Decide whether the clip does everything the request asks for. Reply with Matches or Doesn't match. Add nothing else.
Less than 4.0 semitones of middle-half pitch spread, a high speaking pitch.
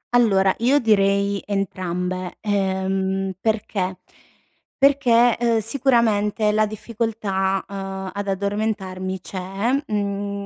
Matches